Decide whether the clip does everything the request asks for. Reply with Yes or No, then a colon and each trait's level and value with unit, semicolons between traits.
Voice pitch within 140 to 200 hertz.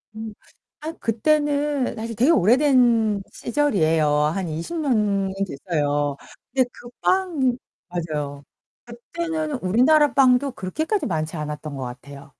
No: high, 225 Hz